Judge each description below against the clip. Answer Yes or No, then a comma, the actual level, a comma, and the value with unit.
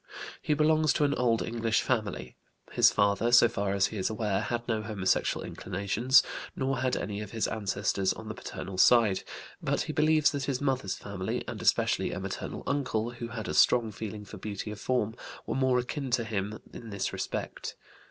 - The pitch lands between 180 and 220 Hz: No, low, 110 Hz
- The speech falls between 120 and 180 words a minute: No, average, 190 wpm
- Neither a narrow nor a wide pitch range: Yes, average, 3.7 semitones